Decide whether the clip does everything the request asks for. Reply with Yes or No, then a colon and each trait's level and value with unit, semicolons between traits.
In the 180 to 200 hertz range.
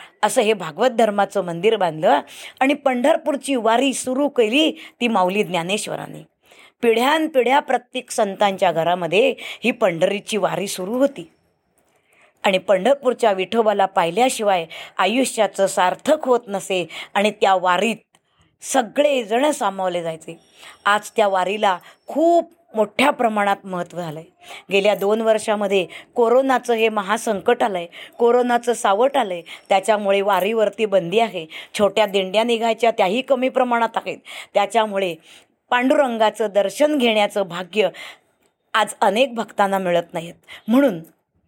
No: high, 215 Hz